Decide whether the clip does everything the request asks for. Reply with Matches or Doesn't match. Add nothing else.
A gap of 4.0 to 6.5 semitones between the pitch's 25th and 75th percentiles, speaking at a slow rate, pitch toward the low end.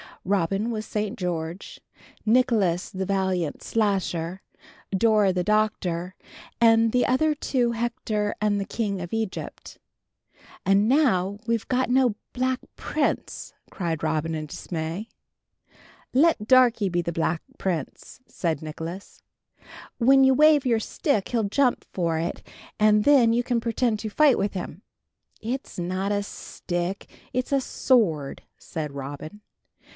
Doesn't match